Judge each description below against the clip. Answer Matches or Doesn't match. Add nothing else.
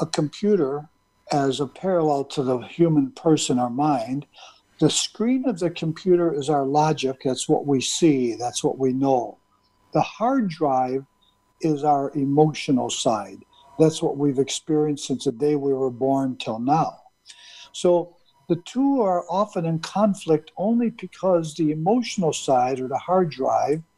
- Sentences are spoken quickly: Doesn't match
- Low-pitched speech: Doesn't match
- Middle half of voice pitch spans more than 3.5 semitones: Matches